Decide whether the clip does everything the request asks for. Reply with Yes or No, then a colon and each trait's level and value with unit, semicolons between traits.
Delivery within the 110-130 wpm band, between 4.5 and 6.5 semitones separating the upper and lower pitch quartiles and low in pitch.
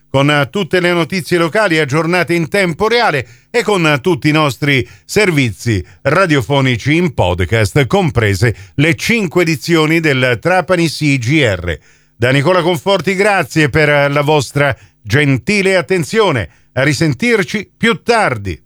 No: average, 120 wpm; wide, 5.4 semitones; medium, 155 Hz